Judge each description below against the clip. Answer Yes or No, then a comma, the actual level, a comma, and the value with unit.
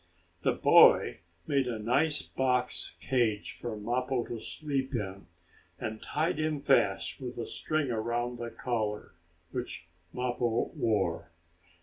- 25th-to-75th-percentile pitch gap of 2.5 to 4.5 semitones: Yes, average, 3.4 semitones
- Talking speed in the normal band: No, slow, 125 wpm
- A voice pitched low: Yes, low, 120 Hz